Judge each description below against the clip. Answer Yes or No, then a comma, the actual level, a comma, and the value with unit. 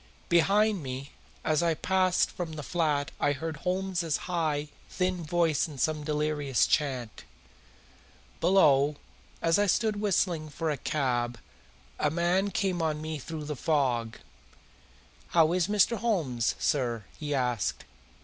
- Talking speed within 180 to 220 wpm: No, slow, 135 wpm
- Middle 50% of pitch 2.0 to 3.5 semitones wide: No, average, 3.9 semitones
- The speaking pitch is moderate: Yes, medium, 155 Hz